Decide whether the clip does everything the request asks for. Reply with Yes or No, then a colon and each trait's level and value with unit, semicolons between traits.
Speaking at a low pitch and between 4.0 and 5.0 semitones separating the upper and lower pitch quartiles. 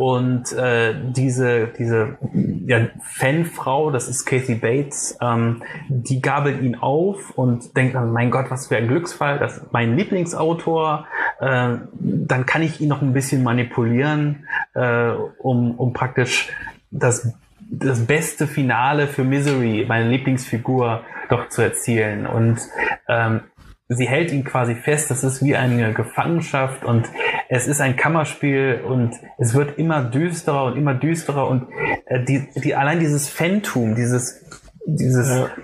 No: low, 130 Hz; average, 3.3 semitones